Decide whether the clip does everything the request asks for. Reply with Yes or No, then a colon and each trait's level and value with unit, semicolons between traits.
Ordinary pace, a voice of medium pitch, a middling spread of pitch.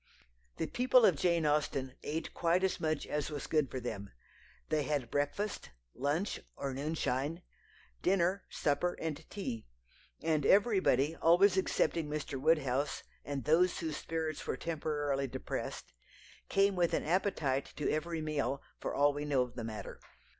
Yes: average, 150 wpm; medium, 155 Hz; average, 3.5 semitones